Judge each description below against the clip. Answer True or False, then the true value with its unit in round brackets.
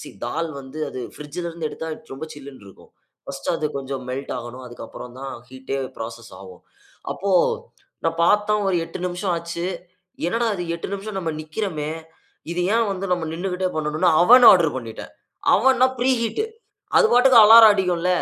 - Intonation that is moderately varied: False (6.2 semitones)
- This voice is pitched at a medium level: True (170 Hz)